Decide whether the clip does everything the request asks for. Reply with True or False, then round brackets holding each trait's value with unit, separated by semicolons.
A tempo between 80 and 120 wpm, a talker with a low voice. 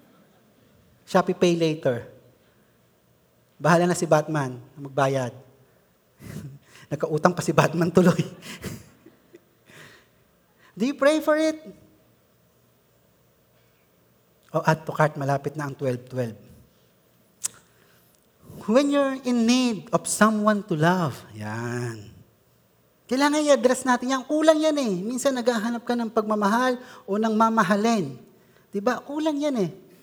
False (110 wpm; 180 Hz)